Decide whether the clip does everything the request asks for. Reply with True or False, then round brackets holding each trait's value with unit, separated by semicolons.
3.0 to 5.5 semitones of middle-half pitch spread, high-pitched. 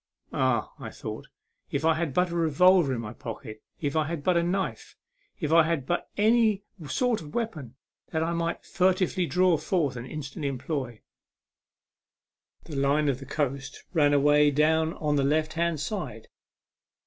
False (3.7 semitones; 155 Hz)